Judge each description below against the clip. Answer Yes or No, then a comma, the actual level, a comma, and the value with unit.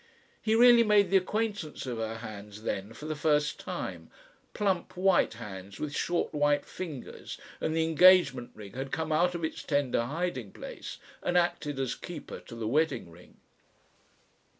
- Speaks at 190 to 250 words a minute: No, average, 165 wpm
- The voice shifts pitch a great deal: Yes, wide, 7.3 semitones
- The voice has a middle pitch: Yes, medium, 150 Hz